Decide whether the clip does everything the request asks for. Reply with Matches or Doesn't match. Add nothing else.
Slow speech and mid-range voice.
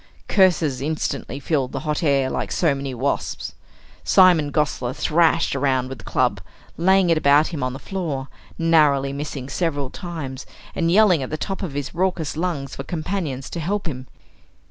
Doesn't match